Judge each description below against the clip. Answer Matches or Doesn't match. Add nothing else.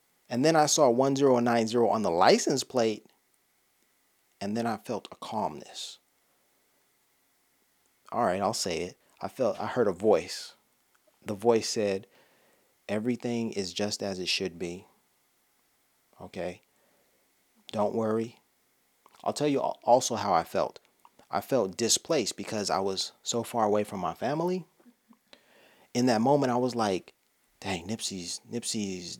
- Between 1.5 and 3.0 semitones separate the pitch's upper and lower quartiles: Doesn't match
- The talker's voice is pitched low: Matches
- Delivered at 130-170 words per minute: Matches